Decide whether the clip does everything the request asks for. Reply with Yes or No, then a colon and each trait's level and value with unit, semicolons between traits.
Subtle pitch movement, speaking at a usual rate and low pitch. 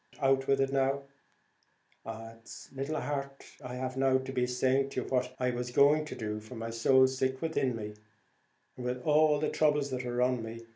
Yes: narrow, 1.8 semitones; average, 195 wpm; low, 130 Hz